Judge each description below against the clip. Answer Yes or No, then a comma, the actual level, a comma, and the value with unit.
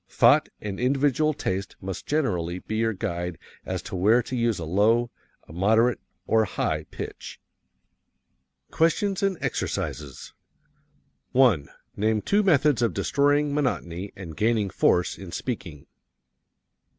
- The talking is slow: Yes, slow, 130 wpm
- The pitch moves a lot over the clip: Yes, wide, 6.8 semitones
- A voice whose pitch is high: No, low, 110 Hz